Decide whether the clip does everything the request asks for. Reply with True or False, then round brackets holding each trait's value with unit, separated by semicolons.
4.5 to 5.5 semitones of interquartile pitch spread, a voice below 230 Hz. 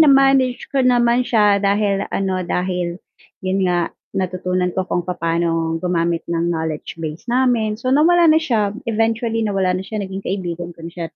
True (4.8 semitones; 190 Hz)